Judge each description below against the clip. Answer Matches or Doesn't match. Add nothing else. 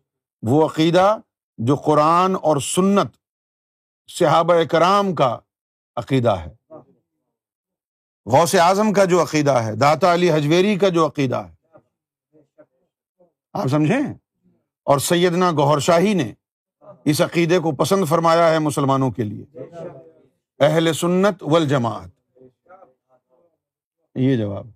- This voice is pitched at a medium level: Matches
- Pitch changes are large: Doesn't match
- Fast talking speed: Doesn't match